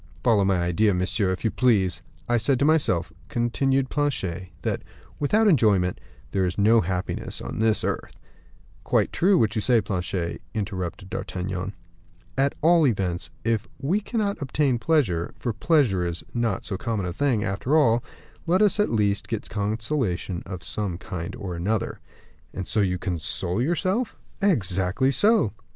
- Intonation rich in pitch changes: Yes, wide, 6.7 semitones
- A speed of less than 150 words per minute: No, average, 155 wpm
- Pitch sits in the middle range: No, low, 110 Hz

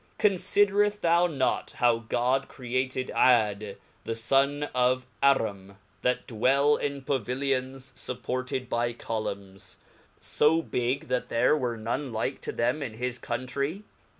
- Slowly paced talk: Yes, slow, 125 wpm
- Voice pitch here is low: Yes, low, 130 Hz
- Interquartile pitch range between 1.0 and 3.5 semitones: Yes, average, 2.8 semitones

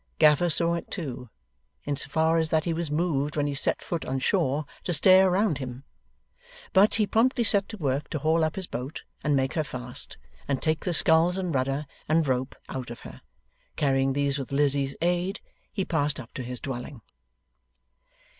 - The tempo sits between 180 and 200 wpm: Yes, average, 190 wpm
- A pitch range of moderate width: Yes, average, 4.1 semitones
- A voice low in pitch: No, medium, 150 Hz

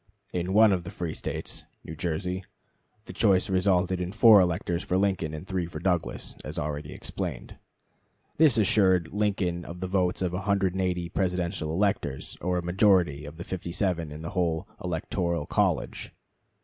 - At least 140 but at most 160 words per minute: Yes, average, 155 wpm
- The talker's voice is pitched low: Yes, very low, 90 Hz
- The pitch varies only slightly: Yes, narrow, 2.1 semitones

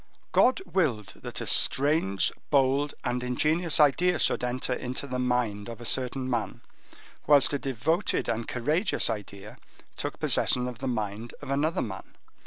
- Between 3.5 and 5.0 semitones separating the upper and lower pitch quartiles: Yes, average, 4.0 semitones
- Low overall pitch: Yes, low, 125 Hz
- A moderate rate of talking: Yes, average, 155 wpm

